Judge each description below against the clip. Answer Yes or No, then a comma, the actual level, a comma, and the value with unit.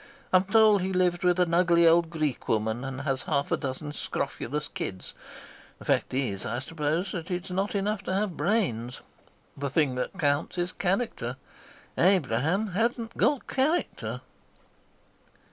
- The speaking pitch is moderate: Yes, medium, 170 Hz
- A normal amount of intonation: No, wide, 5.8 semitones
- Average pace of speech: Yes, average, 150 wpm